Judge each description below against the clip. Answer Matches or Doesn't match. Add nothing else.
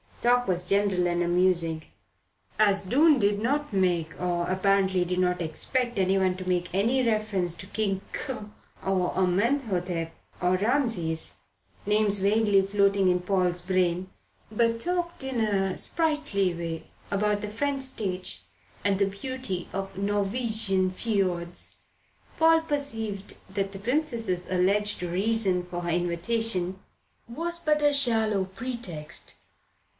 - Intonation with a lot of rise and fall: Doesn't match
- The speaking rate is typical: Doesn't match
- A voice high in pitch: Matches